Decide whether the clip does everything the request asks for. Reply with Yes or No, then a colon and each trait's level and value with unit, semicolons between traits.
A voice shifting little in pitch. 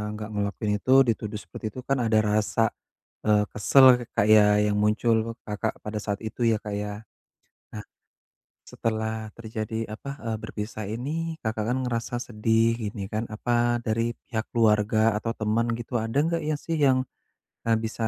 Yes: narrow, 1.5 semitones